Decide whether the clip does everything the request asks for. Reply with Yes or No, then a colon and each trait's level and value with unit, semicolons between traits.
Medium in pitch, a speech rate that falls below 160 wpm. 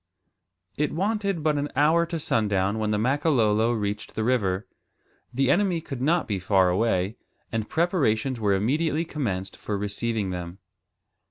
No: low, 115 Hz; average, 150 wpm